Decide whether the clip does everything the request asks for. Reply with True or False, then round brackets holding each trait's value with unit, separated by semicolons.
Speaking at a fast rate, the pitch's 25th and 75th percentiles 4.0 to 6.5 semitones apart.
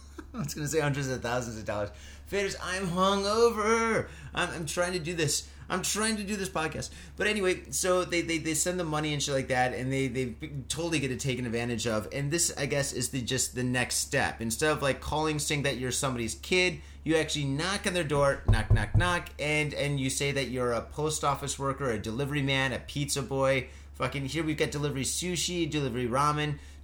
True (220 wpm; 4.7 semitones)